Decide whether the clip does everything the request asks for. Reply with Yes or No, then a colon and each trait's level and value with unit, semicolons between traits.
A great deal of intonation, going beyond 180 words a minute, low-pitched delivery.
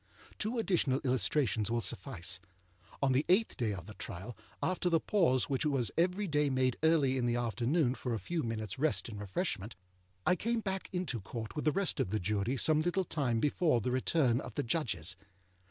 Yes: wide, 6.5 semitones; average, 195 wpm; low, 130 Hz